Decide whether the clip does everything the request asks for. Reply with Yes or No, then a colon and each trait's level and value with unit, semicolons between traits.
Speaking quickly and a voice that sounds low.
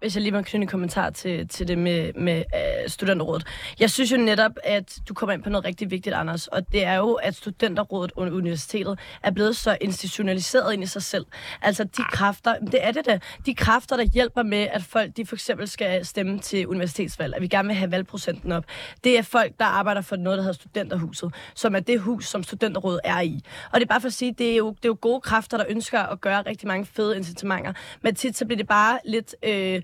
No: fast, 240 wpm; high, 205 Hz